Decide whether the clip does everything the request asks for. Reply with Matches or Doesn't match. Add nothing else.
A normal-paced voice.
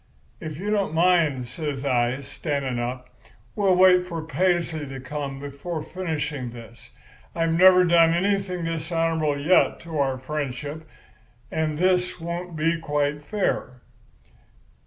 Doesn't match